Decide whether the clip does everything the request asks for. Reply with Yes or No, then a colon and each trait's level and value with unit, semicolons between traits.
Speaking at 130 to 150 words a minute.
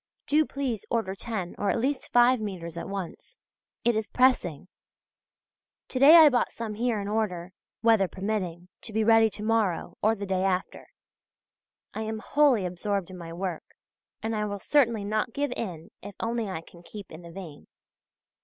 No: average, 180 wpm